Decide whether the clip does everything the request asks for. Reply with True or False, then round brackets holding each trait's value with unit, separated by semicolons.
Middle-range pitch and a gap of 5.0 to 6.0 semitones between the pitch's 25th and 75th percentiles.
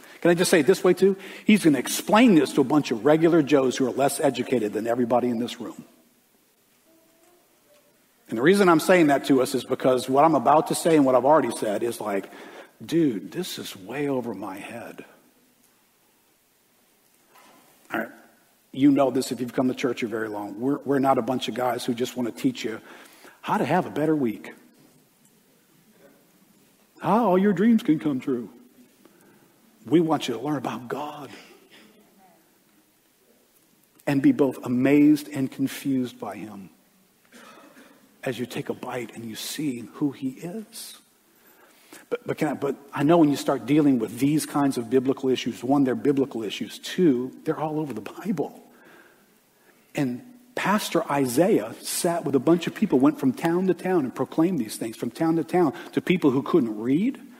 True (145 Hz; 5.5 semitones)